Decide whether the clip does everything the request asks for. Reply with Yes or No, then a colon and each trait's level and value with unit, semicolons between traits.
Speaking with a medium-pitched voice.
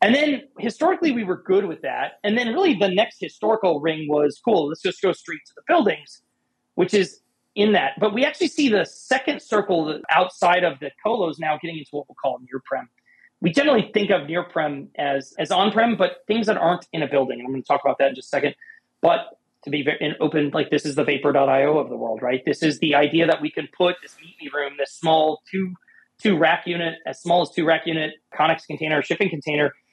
Yes: medium, 165 Hz